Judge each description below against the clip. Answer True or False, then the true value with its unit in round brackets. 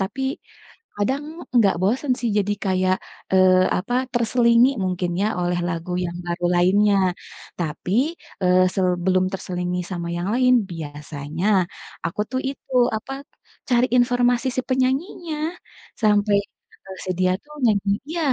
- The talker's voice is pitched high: True (195 Hz)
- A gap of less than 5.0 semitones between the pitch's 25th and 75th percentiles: False (5.5 semitones)